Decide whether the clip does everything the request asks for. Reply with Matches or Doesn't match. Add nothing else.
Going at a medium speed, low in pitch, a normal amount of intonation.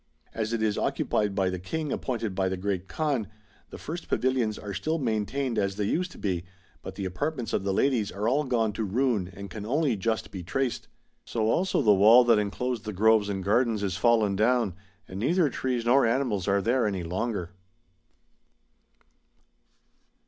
Matches